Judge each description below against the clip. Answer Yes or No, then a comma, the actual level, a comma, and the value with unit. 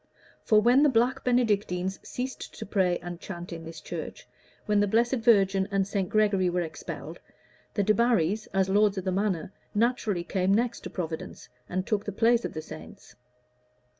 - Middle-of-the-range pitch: No, high, 200 Hz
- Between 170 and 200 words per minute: Yes, average, 175 wpm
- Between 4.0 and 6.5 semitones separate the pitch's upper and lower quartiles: No, average, 3.6 semitones